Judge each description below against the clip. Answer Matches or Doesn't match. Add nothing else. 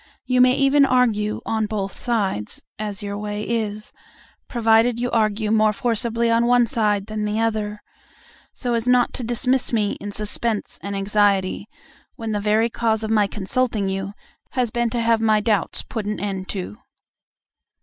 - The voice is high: Matches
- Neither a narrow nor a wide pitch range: Doesn't match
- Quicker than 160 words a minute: Matches